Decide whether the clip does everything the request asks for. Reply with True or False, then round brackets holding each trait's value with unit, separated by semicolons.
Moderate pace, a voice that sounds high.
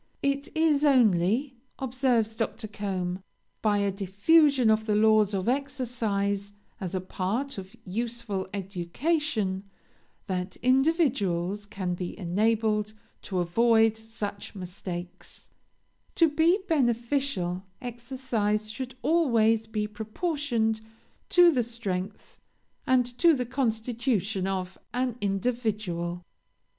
False (105 wpm; 220 Hz)